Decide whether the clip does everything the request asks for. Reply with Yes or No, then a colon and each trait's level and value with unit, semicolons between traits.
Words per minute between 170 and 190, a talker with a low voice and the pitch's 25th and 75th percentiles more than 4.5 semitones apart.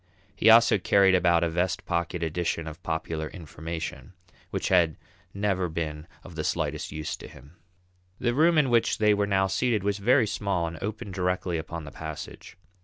No: average, 180 wpm; very low, 90 Hz; average, 3.9 semitones